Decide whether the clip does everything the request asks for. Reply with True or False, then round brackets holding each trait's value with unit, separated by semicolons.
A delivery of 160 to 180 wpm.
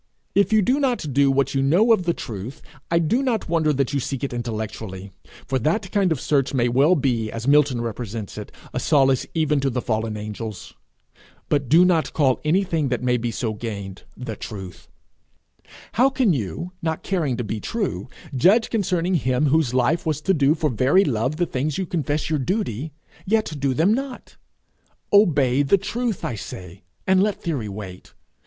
False (190 wpm)